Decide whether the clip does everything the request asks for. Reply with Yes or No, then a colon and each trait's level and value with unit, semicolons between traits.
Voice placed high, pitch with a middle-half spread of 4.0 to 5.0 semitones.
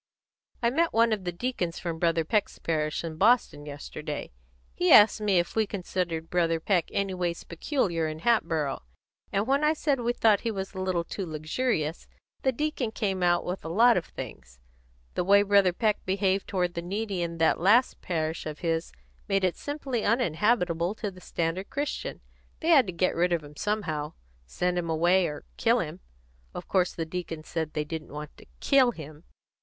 No: medium, 180 Hz; average, 4.6 semitones